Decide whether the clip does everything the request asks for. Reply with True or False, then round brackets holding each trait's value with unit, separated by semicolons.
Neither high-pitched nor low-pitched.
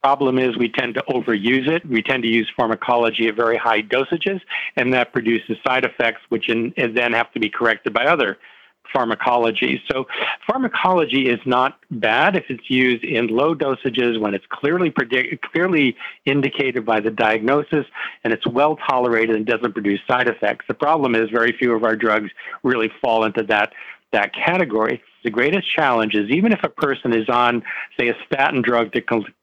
False (120 Hz)